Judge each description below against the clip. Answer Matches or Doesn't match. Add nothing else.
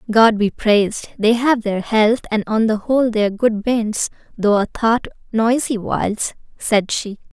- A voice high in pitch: Matches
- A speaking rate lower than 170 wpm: Doesn't match